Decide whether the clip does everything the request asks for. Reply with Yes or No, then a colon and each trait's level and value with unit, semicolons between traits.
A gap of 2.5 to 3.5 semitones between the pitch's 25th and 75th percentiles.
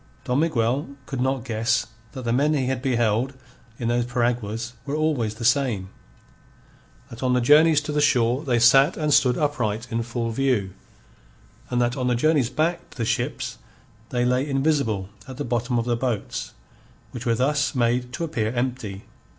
Yes: average, 3.0 semitones